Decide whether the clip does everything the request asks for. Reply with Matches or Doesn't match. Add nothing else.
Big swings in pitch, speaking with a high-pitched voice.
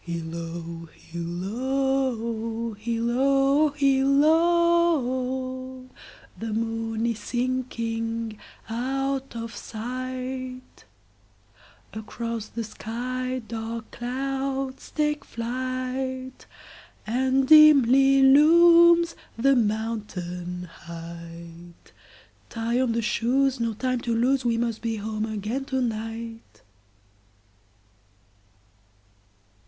Doesn't match